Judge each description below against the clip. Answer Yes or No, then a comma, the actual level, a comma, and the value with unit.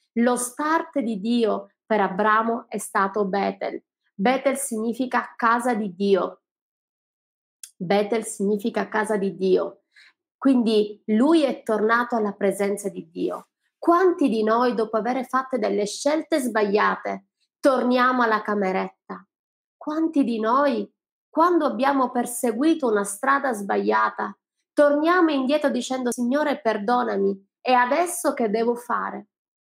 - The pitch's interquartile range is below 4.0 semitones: No, average, 4.5 semitones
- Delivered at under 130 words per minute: Yes, slow, 115 wpm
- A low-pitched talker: No, high, 235 Hz